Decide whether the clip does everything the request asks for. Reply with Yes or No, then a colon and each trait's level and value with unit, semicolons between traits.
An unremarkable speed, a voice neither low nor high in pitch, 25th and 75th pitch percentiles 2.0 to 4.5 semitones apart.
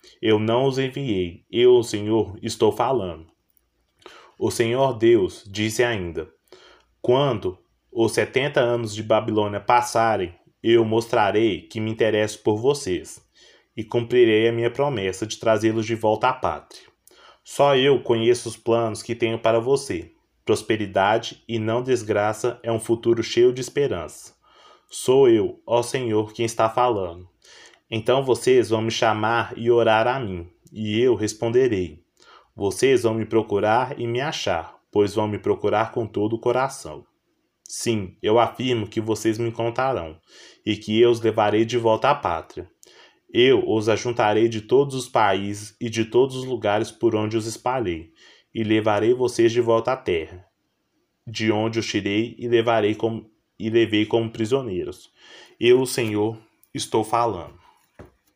No: average, 150 wpm; low, 115 Hz; narrow, 2.5 semitones